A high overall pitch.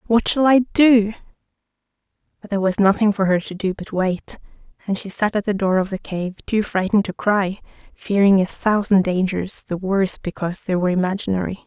Yes: high, 200 Hz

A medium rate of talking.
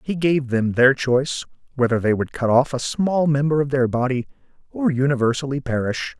Yes: average, 185 wpm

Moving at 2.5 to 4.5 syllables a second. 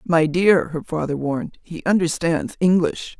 Yes: 4.4 syllables/s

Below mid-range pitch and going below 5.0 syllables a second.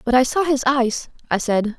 No: very high, 250 Hz; 4.8 syllables/s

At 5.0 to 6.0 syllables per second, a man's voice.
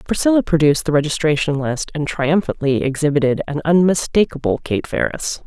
No: 5.7 syllables/s; female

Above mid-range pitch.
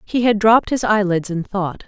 Yes: high, 205 Hz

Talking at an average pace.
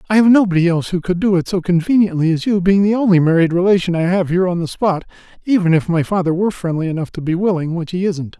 No: fast, 255 wpm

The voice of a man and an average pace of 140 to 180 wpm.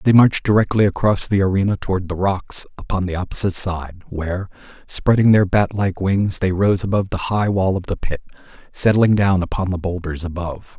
No: male; average, 190 wpm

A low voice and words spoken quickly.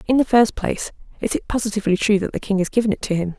No: high, 210 Hz; fast, 285 wpm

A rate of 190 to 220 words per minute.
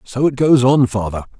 Yes: fast, 215 wpm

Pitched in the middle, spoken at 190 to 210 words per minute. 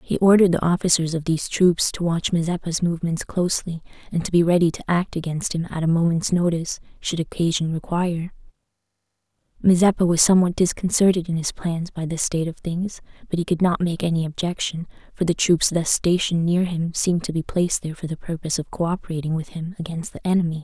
Yes: medium, 170 Hz; average, 200 wpm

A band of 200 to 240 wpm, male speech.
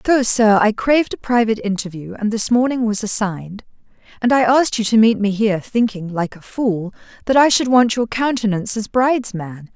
No: fast, 205 wpm; female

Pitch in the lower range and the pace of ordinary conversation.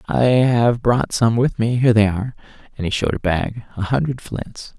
Yes: low, 115 Hz; average, 190 wpm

